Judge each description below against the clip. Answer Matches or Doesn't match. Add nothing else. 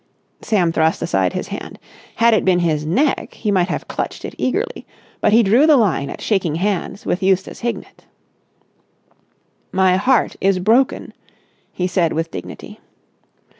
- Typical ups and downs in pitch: Matches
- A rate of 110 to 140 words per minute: Doesn't match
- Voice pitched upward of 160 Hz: Matches